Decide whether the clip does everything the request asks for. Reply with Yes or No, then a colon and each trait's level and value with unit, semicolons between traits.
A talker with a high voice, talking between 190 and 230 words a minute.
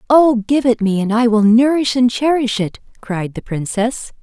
Yes: high, 235 Hz; average, 200 wpm